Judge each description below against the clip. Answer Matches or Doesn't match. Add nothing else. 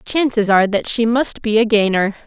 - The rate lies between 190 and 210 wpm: Doesn't match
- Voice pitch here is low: Doesn't match